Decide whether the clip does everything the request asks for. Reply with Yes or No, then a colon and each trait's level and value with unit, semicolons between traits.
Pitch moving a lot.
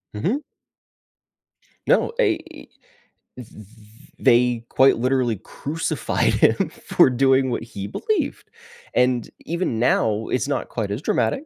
No: average, 3.3 semitones